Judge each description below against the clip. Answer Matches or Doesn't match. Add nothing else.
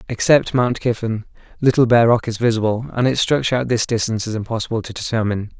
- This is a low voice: Matches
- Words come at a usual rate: Matches